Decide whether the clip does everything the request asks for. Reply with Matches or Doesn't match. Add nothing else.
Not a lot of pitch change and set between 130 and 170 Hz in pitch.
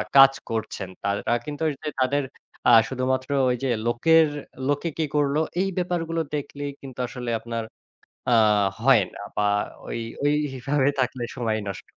Doesn't match